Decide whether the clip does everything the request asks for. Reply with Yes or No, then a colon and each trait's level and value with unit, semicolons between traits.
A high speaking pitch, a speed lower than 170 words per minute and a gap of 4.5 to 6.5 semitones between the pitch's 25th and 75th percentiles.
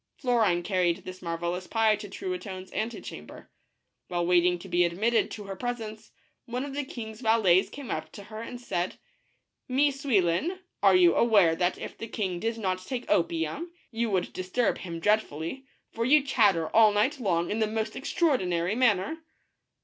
No: high, 210 Hz; average, 175 wpm; average, 5.1 semitones